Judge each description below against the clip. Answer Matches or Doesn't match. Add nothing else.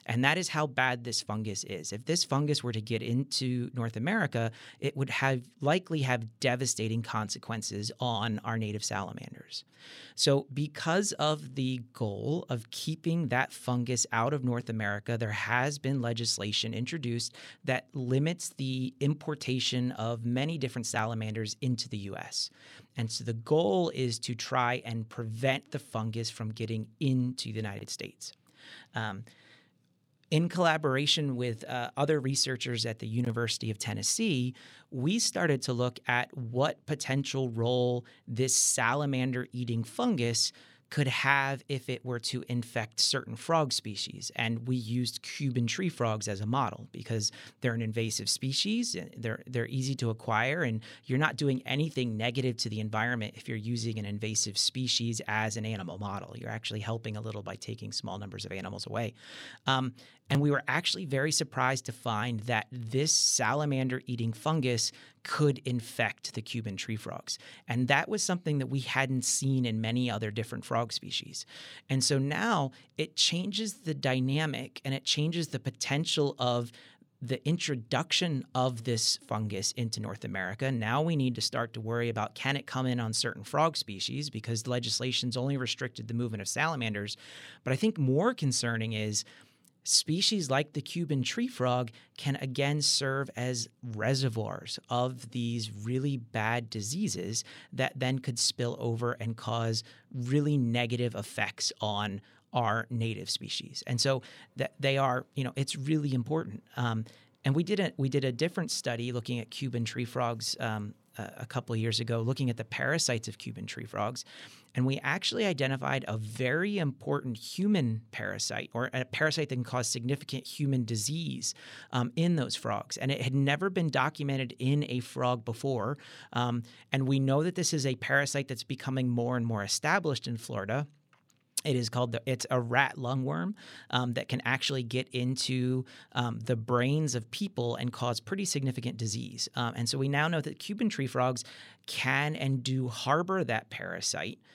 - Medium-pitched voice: Doesn't match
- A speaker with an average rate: Matches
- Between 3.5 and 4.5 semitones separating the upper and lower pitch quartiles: Doesn't match